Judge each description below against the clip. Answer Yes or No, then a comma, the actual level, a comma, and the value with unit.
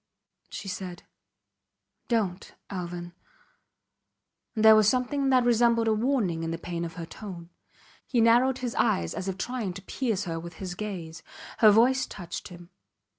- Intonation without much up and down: No, average, 5.2 semitones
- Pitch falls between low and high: No, high, 200 Hz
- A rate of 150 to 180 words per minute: Yes, average, 160 wpm